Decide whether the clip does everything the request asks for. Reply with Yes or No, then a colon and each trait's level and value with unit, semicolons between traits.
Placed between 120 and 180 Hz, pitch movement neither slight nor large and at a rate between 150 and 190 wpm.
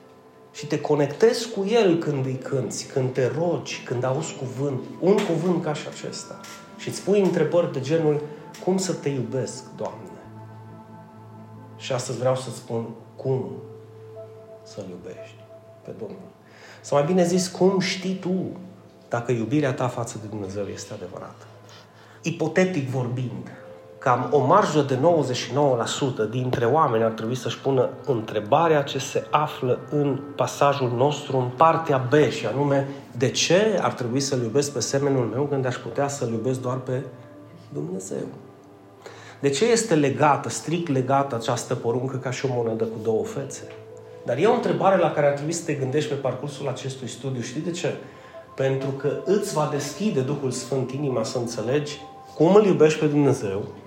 Yes: low, 135 Hz; average, 4.3 semitones; average, 160 wpm